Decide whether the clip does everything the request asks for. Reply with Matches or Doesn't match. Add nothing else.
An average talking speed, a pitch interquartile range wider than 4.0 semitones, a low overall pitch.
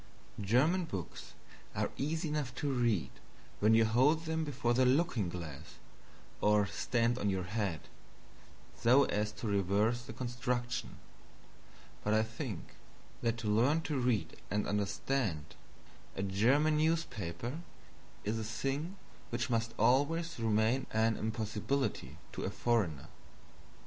Doesn't match